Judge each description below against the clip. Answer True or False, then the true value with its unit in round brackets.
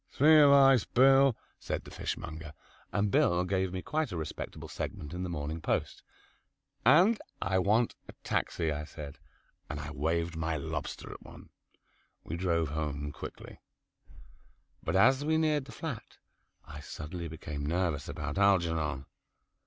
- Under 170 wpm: True (150 wpm)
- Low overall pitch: True (90 Hz)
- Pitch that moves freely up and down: True (8.2 semitones)